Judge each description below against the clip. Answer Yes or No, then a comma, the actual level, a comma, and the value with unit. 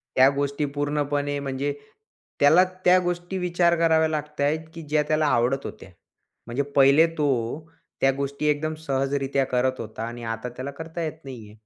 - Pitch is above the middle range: No, medium, 145 Hz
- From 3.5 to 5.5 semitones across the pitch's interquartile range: No, average, 2.7 semitones